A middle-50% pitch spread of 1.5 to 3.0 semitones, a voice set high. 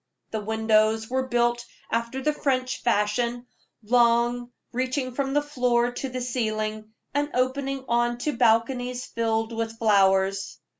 Yes: narrow, 2.5 semitones; high, 240 Hz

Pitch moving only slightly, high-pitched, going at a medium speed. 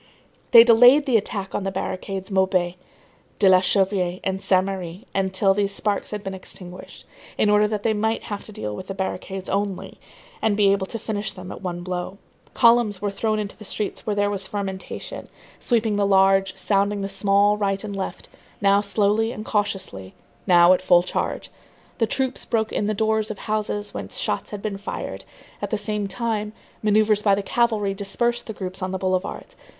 Yes: narrow, 2.0 semitones; high, 200 Hz; average, 190 wpm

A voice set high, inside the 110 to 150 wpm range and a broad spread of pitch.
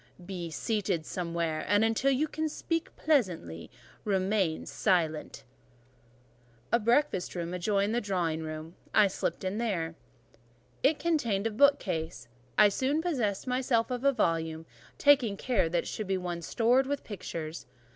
Yes: high, 200 Hz; average, 145 wpm; wide, 6.8 semitones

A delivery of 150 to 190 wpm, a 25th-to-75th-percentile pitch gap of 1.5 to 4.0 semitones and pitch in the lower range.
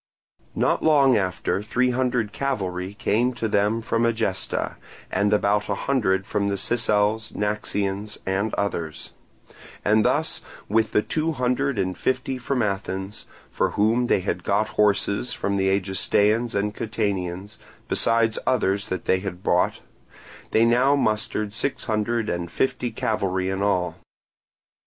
No: average, 140 wpm; average, 3.0 semitones; low, 105 Hz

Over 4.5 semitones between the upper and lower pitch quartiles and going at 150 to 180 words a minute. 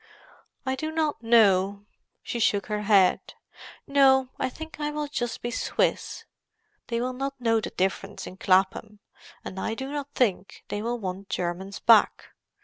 Yes: average, 5.1 semitones; average, 160 wpm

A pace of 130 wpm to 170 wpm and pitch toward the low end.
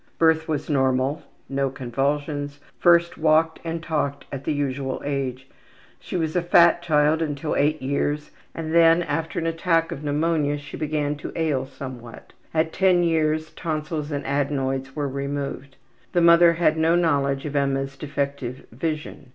No: average, 155 wpm; medium, 150 Hz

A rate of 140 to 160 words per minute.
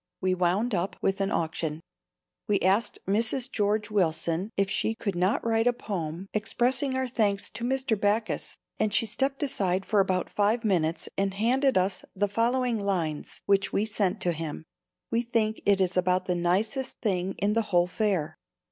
No: average, 175 wpm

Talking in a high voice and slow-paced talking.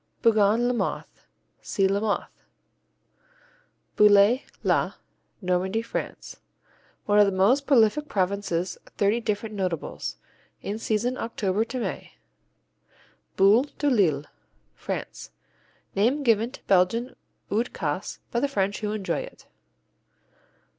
Yes: high, 210 Hz; slow, 110 wpm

